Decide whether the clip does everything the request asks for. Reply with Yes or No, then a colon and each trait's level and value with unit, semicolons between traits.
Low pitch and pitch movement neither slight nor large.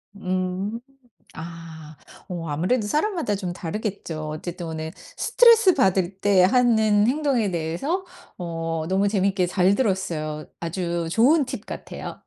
No: medium, 185 Hz; average, 4.7 semitones